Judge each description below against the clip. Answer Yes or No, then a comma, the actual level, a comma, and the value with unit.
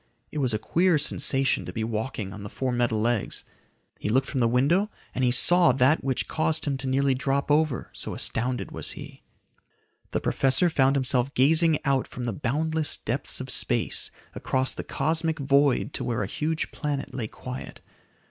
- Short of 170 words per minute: No, average, 185 wpm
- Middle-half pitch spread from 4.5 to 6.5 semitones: No, average, 3.5 semitones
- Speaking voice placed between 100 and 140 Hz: Yes, low, 135 Hz